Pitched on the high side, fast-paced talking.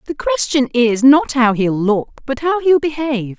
No: very high, 260 Hz; average, 195 wpm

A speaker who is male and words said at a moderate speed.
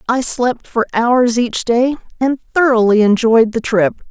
No: female; average, 160 wpm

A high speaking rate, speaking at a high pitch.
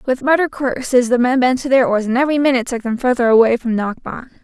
Yes: fast, 245 wpm; very high, 250 Hz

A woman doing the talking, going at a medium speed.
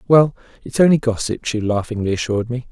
No: male; average, 175 wpm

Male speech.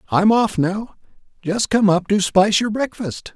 Yes: male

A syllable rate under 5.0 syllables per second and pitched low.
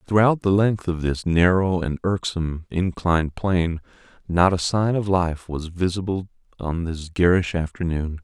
Yes: 4.6 syllables/s; very low, 90 Hz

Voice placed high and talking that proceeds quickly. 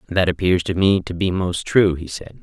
No: very low, 90 Hz; fast, 245 wpm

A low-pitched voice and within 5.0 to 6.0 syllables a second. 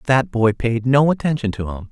Yes: low, 125 Hz; 5.7 syllables/s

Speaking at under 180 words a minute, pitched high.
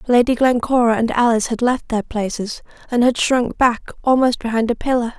No: average, 185 wpm; high, 240 Hz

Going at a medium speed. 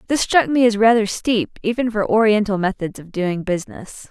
Yes: average, 190 wpm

